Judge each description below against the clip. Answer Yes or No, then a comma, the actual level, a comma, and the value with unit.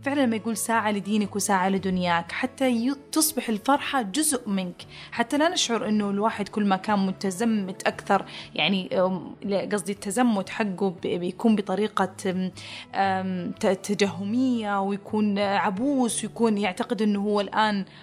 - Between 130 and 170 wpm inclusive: No, average, 120 wpm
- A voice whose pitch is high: Yes, high, 205 Hz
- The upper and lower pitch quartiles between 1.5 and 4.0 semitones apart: Yes, average, 3.2 semitones